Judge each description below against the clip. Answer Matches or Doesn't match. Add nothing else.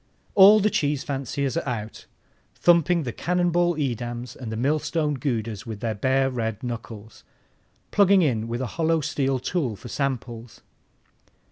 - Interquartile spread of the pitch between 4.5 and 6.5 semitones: Matches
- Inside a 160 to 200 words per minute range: Doesn't match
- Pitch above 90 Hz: Matches